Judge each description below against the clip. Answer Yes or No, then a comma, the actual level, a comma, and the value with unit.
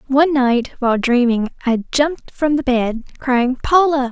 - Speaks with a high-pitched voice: Yes, very high, 260 Hz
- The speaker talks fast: No, average, 160 wpm